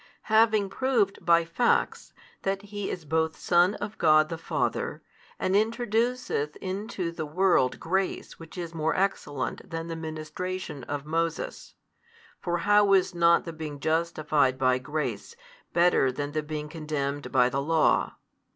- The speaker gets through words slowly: No, average, 145 wpm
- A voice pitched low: No, medium, 165 Hz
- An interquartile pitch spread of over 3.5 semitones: Yes, average, 4.1 semitones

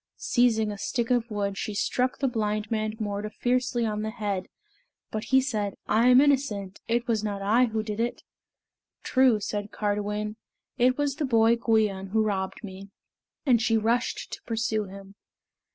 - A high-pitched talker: Yes, high, 220 Hz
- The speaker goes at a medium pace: Yes, average, 170 wpm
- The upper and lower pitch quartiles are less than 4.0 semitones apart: Yes, narrow, 2.6 semitones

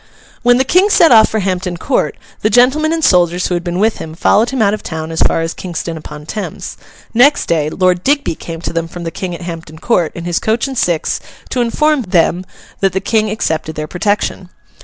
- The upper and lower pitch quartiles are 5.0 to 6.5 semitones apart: Yes, wide, 5.6 semitones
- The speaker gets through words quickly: Yes, fast, 225 wpm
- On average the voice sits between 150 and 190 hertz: Yes, medium, 185 Hz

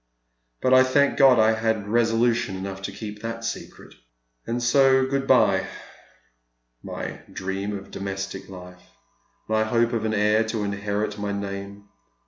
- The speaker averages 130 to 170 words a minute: Yes, average, 145 wpm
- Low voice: Yes, low, 110 Hz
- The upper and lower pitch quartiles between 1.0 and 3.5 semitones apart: Yes, average, 2.8 semitones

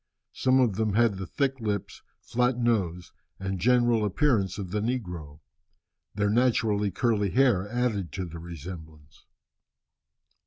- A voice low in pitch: Yes, low, 105 Hz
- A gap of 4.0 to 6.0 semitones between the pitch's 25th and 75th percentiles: Yes, average, 4.8 semitones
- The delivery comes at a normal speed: No, slow, 130 wpm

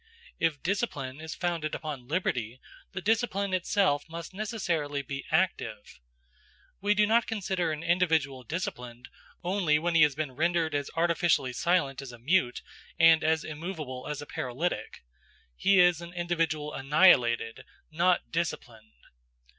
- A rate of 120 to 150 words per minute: Yes, average, 140 wpm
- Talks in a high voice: No, medium, 160 Hz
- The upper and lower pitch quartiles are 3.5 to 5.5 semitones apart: Yes, average, 4.2 semitones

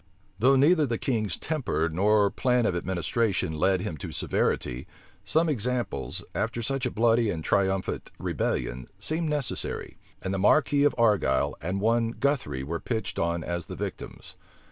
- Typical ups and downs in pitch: No, wide, 5.9 semitones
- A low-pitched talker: Yes, low, 110 Hz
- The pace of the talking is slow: No, average, 155 wpm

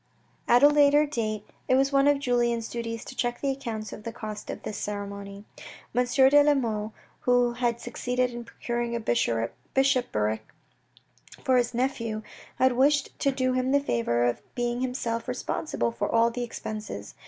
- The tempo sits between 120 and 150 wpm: No, average, 170 wpm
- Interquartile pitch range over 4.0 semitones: No, average, 3.3 semitones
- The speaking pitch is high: Yes, high, 240 Hz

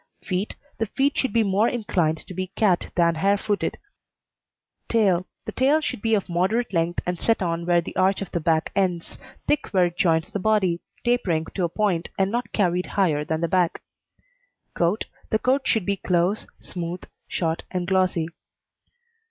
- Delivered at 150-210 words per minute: Yes, average, 180 wpm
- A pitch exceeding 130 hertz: Yes, medium, 185 Hz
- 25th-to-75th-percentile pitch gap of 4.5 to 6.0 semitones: No, average, 3.6 semitones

